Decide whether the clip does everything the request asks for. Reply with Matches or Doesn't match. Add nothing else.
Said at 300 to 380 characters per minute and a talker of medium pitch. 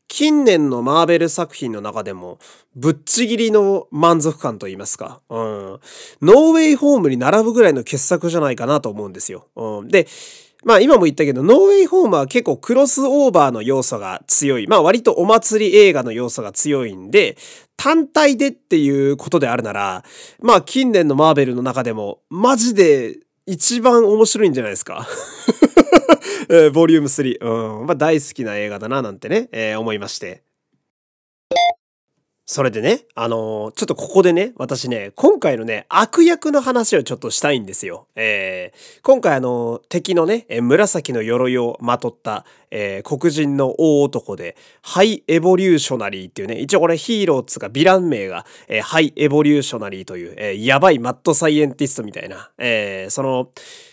Matches